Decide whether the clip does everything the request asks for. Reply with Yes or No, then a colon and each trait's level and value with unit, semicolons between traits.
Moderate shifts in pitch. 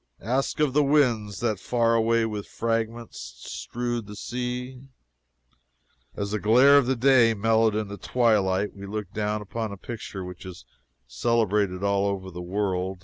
Yes: average, 3.1 semitones